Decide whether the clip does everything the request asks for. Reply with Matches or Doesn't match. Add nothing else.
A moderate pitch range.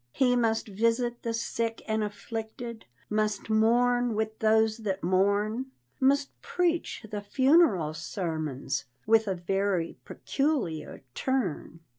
Matches